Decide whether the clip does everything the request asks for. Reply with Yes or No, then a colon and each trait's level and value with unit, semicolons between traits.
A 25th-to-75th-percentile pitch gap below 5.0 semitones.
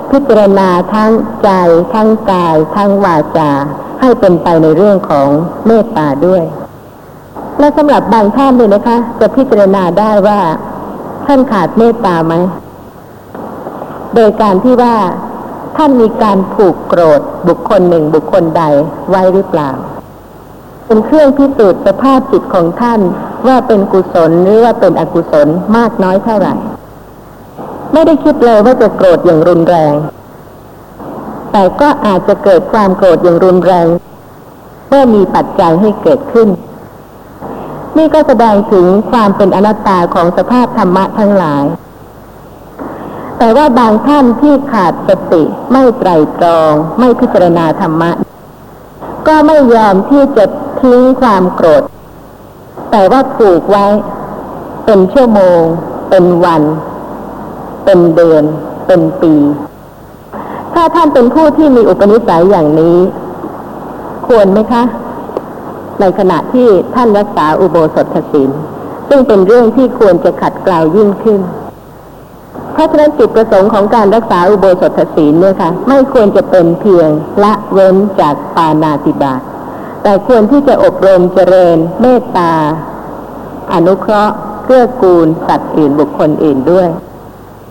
No: wide, 5.6 semitones